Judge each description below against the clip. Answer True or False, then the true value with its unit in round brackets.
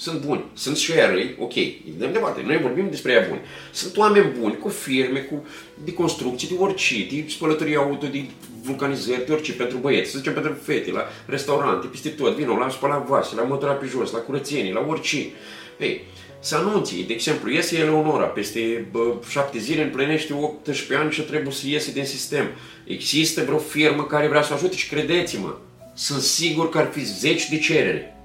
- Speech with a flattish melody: True (2.2 semitones)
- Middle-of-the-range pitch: True (150 Hz)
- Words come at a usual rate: False (185 wpm)